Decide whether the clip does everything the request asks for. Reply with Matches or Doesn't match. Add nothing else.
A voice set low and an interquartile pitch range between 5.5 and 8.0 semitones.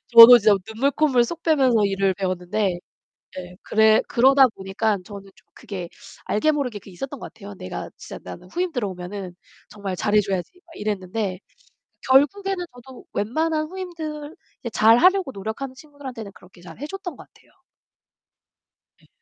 Doesn't match